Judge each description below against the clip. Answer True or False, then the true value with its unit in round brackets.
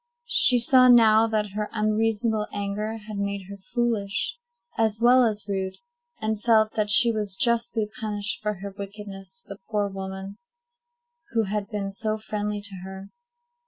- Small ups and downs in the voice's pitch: True (1.9 semitones)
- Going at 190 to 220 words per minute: False (160 wpm)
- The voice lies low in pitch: False (210 Hz)